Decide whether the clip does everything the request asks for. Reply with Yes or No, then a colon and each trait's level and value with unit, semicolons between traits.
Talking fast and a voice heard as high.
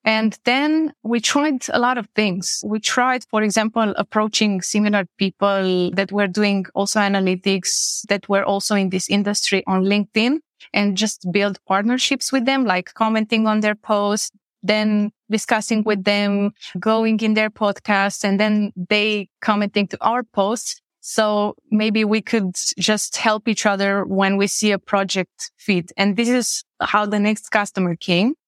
No: average, 160 wpm; high, 210 Hz